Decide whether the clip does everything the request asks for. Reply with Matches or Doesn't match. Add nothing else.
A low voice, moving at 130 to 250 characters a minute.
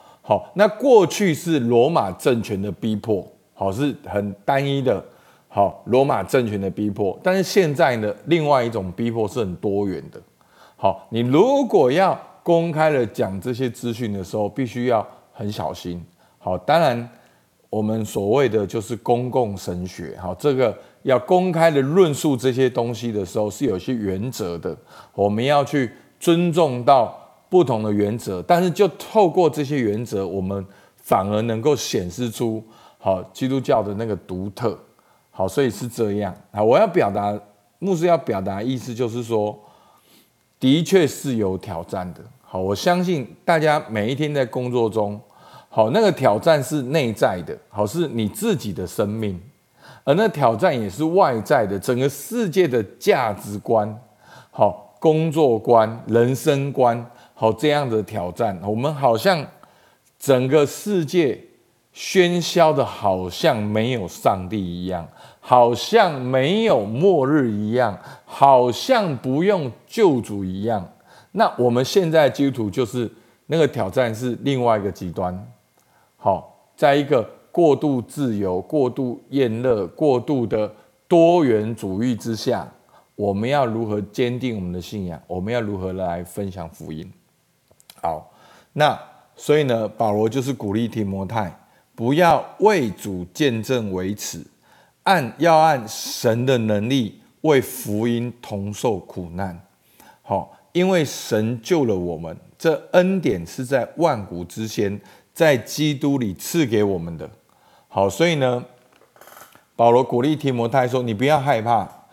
Matches